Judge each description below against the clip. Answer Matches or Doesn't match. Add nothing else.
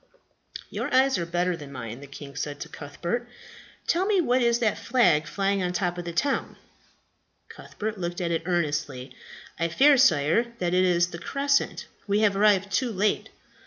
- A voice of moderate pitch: Matches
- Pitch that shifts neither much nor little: Doesn't match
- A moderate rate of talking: Matches